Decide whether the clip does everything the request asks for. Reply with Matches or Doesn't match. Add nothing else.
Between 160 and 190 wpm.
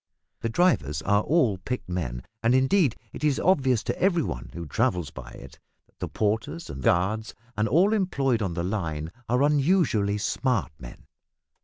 Matches